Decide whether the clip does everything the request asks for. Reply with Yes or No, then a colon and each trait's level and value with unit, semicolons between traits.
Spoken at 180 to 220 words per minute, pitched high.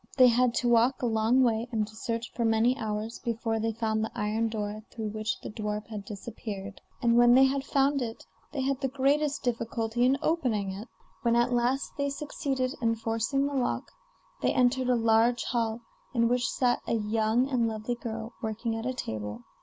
Yes: average, 200 wpm; high, 230 Hz